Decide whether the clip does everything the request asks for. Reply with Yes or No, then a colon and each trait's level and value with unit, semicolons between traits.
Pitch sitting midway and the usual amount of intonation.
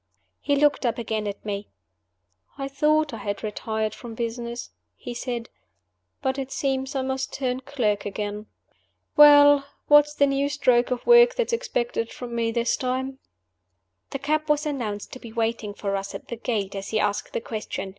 No: high, 245 Hz; average, 4.3 semitones